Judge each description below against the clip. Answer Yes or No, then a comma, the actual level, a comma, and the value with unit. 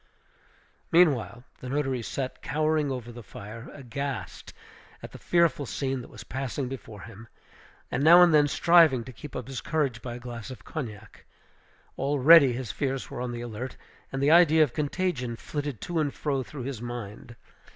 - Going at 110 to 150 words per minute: No, average, 175 wpm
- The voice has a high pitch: No, low, 135 Hz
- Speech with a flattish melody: No, average, 3.7 semitones